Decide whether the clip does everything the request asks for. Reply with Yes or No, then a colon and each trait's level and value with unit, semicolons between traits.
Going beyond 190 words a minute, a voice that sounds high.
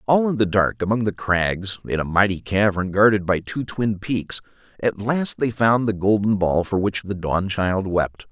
No: average, 200 wpm; low, 100 Hz